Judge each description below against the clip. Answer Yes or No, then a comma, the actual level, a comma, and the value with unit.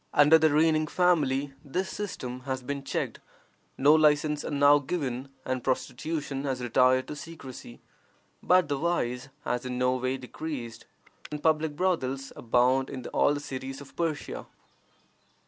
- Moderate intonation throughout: Yes, average, 3.2 semitones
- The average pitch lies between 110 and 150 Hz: Yes, medium, 140 Hz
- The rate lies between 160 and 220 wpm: No, average, 145 wpm